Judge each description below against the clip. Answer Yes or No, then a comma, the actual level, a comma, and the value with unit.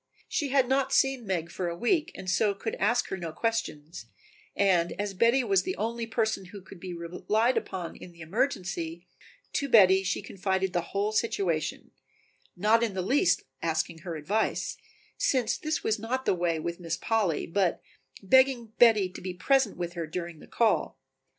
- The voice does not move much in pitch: No, average, 5.0 semitones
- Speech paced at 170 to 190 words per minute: Yes, average, 180 wpm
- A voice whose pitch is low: No, high, 195 Hz